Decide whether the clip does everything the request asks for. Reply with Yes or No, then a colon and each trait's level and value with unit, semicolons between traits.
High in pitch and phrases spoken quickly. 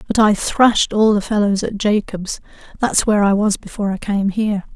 No: high, 205 Hz; average, 190 wpm